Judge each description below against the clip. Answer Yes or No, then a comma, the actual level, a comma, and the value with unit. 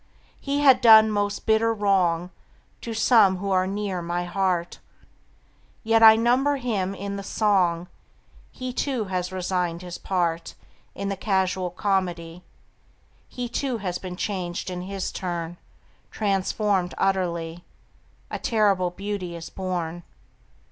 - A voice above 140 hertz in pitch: Yes, high, 190 Hz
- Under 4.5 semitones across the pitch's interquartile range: Yes, average, 3.1 semitones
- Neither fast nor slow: No, slow, 130 wpm